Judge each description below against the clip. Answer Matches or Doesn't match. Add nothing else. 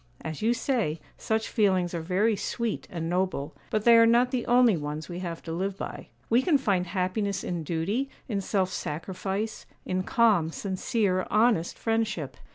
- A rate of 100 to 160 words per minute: Doesn't match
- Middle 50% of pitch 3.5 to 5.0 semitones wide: Matches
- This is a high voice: Matches